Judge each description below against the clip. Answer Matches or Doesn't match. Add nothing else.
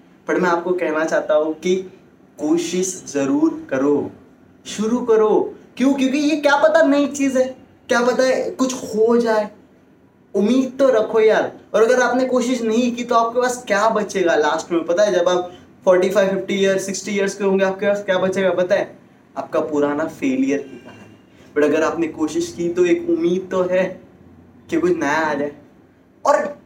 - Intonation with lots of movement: Matches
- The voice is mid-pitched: Doesn't match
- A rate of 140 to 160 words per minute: Doesn't match